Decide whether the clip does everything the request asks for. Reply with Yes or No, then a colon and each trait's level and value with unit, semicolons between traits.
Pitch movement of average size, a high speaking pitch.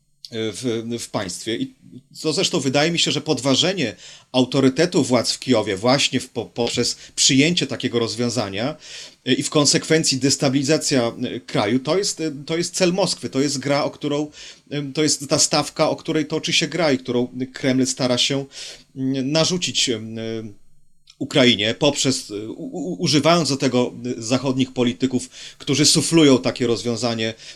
No: average, 3.7 semitones; low, 135 Hz